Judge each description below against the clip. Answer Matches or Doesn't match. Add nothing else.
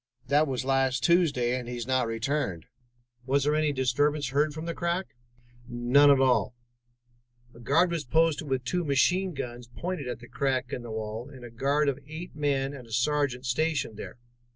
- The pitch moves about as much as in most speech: Matches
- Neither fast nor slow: Matches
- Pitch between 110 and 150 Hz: Matches